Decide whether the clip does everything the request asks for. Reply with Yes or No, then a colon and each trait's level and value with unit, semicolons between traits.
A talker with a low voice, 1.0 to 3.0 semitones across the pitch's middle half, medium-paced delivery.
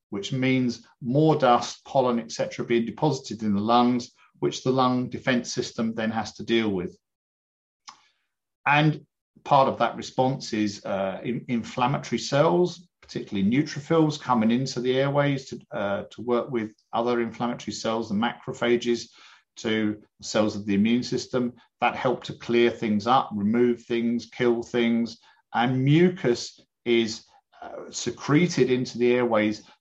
Yes: low, 120 Hz; narrow, 2.5 semitones; average, 145 wpm